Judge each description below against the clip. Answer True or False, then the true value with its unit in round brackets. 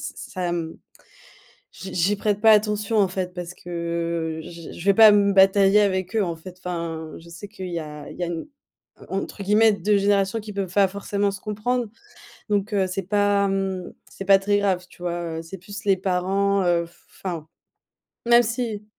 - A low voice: False (195 Hz)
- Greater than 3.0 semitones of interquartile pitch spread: False (2.7 semitones)